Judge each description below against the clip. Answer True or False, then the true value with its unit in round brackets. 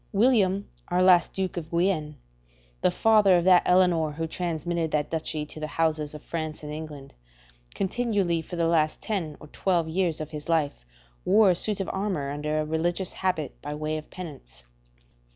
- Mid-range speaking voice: True (165 Hz)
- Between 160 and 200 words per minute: True (180 wpm)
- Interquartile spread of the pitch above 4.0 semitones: False (3.3 semitones)